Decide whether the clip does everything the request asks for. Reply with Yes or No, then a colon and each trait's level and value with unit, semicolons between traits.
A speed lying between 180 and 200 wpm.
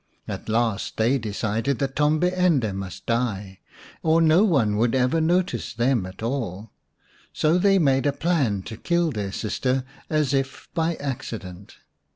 No: average, 155 wpm